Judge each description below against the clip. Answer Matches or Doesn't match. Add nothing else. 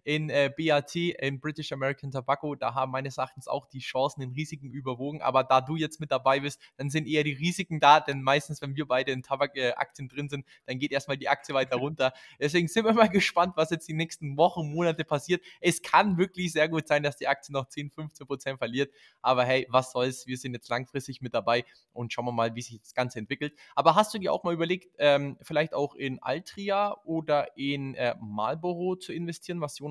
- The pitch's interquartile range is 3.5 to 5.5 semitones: Doesn't match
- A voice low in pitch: Doesn't match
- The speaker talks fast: Matches